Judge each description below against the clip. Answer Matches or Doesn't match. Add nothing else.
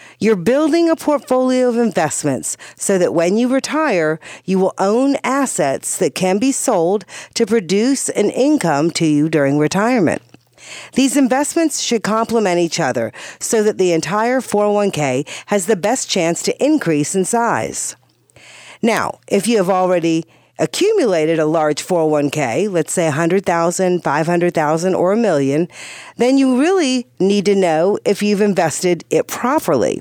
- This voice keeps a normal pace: Matches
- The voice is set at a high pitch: Matches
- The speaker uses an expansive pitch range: Matches